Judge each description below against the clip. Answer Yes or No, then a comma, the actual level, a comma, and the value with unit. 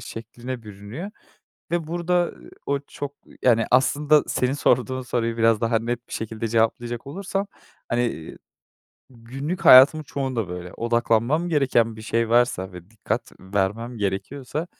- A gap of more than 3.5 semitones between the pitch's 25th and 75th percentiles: Yes, average, 3.9 semitones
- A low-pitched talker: Yes, low, 120 Hz